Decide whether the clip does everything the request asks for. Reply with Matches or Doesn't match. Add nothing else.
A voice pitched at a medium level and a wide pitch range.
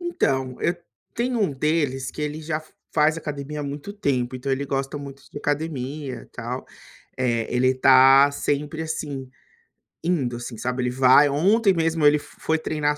Doesn't match